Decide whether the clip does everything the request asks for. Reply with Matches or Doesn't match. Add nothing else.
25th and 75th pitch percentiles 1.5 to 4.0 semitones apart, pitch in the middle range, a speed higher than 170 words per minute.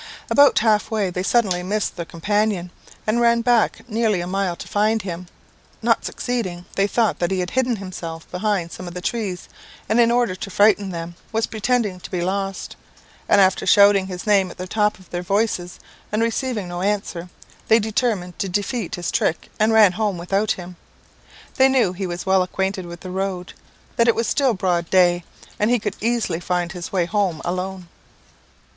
Doesn't match